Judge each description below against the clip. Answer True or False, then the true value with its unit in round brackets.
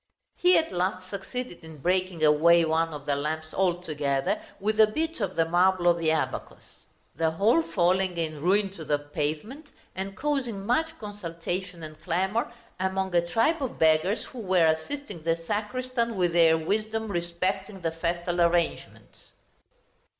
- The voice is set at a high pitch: False (180 Hz)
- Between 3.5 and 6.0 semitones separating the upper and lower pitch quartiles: True (4.2 semitones)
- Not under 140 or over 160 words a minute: True (155 wpm)